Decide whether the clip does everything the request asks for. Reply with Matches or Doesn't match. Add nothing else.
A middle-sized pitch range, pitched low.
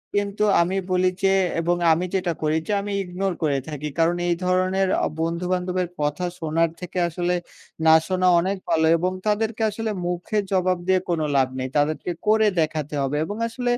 Doesn't match